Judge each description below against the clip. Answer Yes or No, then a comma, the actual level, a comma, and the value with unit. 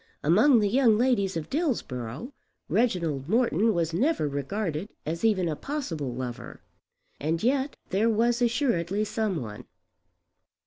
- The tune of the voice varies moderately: No, wide, 7.3 semitones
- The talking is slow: Yes, slow, 130 wpm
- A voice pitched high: Yes, high, 200 Hz